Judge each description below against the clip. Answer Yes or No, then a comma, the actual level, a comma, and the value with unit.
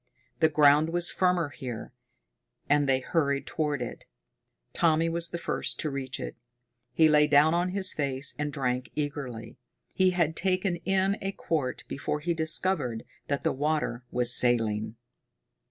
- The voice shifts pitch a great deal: No, average, 4.1 semitones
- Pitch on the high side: No, medium, 150 Hz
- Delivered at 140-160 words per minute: Yes, average, 155 wpm